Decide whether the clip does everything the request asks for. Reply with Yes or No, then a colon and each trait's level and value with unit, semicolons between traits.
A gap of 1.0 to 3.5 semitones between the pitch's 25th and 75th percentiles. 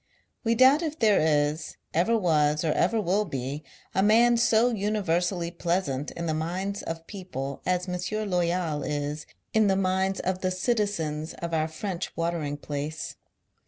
No: average, 4.5 semitones